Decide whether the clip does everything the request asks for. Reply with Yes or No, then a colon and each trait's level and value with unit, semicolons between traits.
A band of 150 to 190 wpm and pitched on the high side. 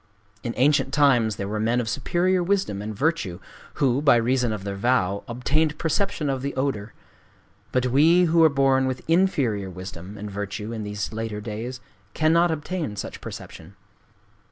No: average, 170 wpm; low, 125 Hz